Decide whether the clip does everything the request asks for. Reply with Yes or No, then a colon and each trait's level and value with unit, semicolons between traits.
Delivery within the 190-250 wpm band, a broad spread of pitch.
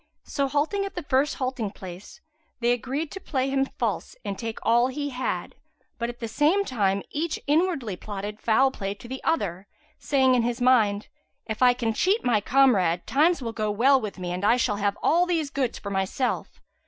No: average, 200 wpm; average, 5.0 semitones